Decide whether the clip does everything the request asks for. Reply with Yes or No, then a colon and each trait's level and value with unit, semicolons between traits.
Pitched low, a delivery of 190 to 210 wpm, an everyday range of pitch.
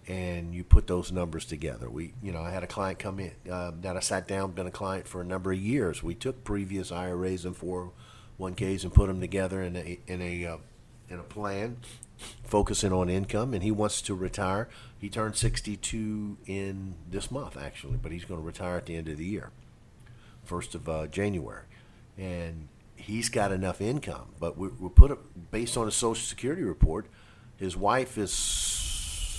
Yes: very low, 95 Hz; average, 200 wpm; average, 3.3 semitones